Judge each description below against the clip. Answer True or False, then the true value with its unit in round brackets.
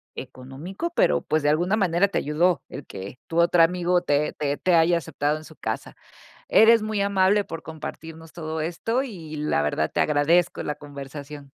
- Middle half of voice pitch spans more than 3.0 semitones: True (3.5 semitones)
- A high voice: False (165 Hz)